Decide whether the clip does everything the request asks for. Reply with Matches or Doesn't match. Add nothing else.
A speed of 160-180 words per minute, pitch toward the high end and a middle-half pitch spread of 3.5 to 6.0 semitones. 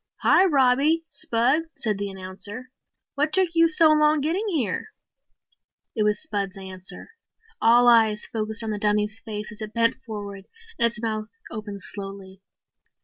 Doesn't match